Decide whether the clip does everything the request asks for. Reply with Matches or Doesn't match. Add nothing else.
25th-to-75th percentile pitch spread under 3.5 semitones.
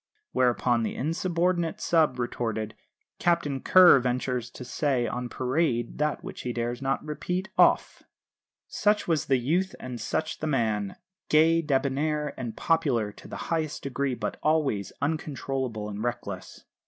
Doesn't match